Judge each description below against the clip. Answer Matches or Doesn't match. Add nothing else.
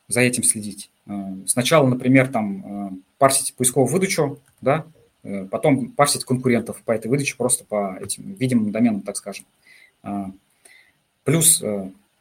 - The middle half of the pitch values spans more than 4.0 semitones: Matches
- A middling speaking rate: Matches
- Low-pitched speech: Matches